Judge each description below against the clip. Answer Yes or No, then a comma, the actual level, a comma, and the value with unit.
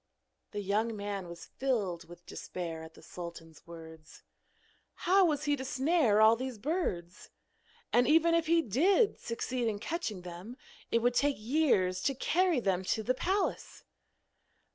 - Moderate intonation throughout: No, wide, 8.2 semitones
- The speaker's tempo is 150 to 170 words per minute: Yes, average, 155 wpm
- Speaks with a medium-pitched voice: No, high, 230 Hz